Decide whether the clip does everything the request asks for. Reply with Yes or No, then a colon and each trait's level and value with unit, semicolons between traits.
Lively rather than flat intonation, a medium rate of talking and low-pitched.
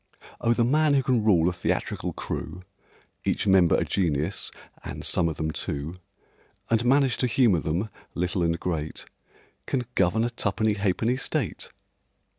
Yes: wide, 6.0 semitones; average, 155 wpm; low, 100 Hz